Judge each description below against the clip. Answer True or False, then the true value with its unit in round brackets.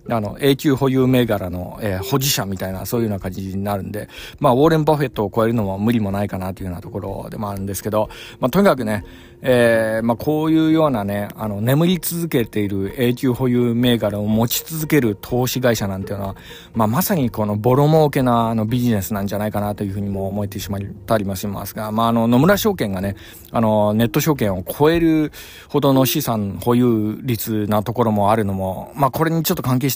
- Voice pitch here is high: False (110 Hz)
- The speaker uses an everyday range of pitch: True (4.3 semitones)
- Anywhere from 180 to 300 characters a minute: False (440 characters per minute)